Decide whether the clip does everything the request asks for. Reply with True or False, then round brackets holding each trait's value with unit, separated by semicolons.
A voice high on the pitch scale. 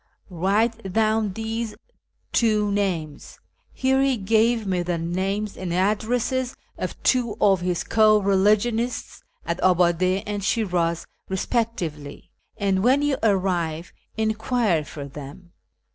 True (200 Hz)